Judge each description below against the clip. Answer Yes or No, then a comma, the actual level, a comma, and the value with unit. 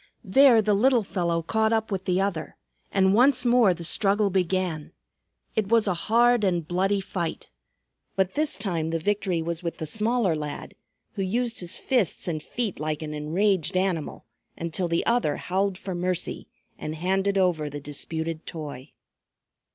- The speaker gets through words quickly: No, average, 165 wpm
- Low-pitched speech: No, medium, 185 Hz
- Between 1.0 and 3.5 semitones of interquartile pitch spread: No, average, 4.2 semitones